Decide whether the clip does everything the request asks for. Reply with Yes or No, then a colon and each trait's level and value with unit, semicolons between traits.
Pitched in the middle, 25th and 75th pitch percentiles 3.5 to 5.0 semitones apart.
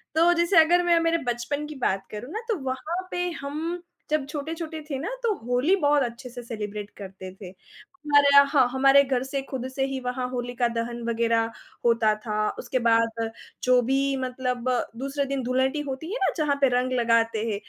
No: very high, 260 Hz; average, 4.0 semitones